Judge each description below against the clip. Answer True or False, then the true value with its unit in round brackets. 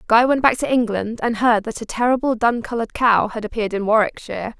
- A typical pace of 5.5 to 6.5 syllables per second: True (6.2 syllables/s)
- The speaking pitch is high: True (230 Hz)